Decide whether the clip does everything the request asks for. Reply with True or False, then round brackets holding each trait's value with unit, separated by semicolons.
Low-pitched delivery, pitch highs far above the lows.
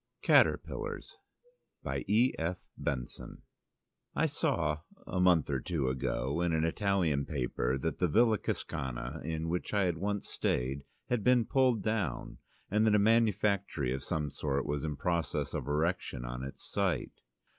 True (80 Hz; 6.3 semitones)